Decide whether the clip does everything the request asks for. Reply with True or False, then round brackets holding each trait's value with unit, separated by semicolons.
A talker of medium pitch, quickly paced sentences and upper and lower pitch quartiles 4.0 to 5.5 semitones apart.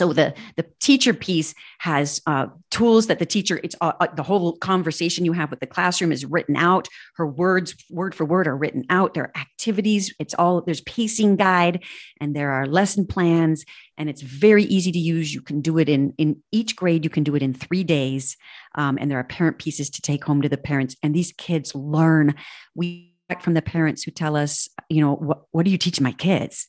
False (165 Hz; 220 wpm; 3.3 semitones)